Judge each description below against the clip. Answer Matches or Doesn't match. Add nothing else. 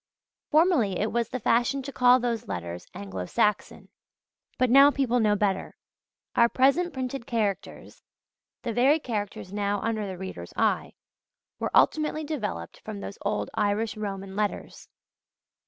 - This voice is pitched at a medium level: Doesn't match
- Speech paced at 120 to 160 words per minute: Matches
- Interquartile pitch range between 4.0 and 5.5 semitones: Matches